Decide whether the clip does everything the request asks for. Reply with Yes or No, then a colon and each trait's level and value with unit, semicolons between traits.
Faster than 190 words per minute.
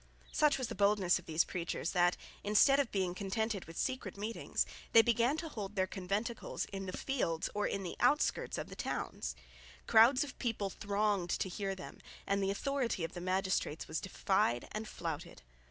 No: average, 185 wpm